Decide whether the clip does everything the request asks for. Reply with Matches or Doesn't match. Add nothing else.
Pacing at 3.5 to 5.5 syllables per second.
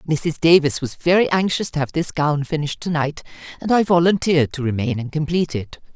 Doesn't match